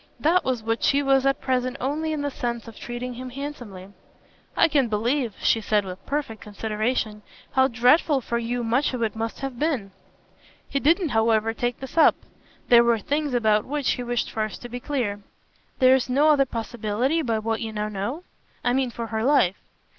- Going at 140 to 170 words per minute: No, average, 190 wpm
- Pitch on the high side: Yes, high, 245 Hz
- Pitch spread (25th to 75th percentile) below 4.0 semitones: Yes, average, 3.5 semitones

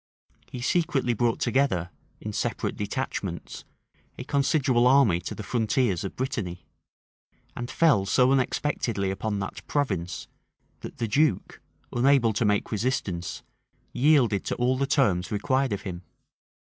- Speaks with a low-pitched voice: Yes, low, 120 Hz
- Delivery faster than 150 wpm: No, slow, 135 wpm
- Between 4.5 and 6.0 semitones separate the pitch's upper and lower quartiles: Yes, average, 5.3 semitones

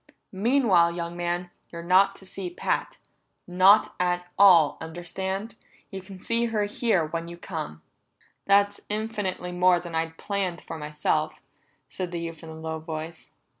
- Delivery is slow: No, average, 155 wpm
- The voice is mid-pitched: Yes, medium, 180 Hz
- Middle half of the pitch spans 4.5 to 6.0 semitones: No, average, 2.8 semitones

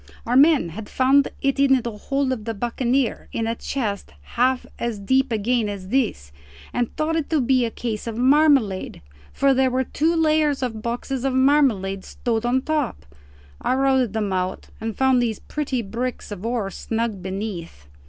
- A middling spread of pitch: Yes, average, 3.8 semitones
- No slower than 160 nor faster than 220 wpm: Yes, average, 180 wpm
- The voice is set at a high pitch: Yes, high, 245 Hz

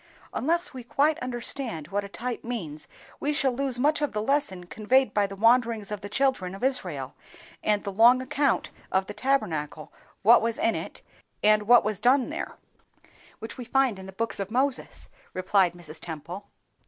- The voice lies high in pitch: Yes, high, 225 Hz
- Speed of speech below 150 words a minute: No, average, 180 wpm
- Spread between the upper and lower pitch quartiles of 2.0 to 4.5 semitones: No, average, 5.1 semitones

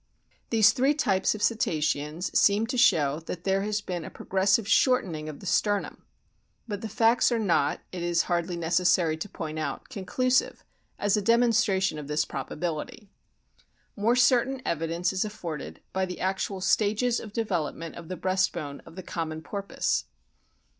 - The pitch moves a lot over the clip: No, average, 4.6 semitones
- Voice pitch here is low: No, high, 190 Hz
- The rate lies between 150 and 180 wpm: Yes, average, 160 wpm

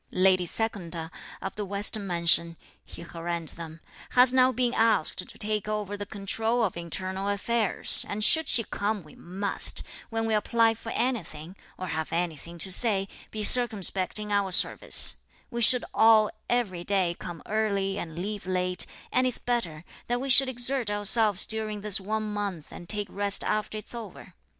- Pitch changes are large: No, average, 3.5 semitones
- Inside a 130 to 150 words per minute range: No, average, 170 wpm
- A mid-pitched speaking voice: No, high, 205 Hz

